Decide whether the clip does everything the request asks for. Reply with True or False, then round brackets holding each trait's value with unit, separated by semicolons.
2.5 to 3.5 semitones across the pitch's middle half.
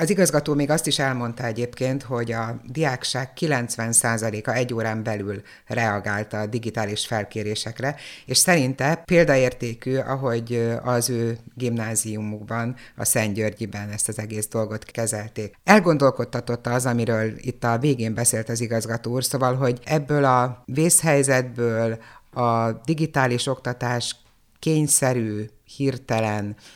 True (2.9 semitones)